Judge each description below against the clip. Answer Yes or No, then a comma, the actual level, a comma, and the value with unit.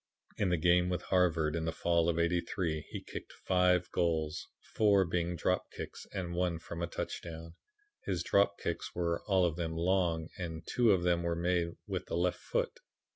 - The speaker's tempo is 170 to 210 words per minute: Yes, average, 185 wpm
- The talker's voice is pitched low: Yes, very low, 85 Hz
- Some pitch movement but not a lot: No, narrow, 1.5 semitones